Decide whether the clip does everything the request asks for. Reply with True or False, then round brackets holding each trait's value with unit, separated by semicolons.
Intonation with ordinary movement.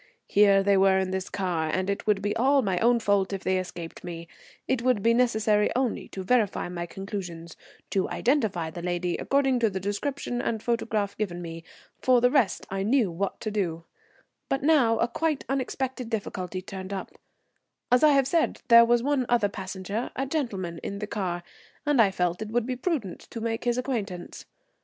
True (4.7 semitones)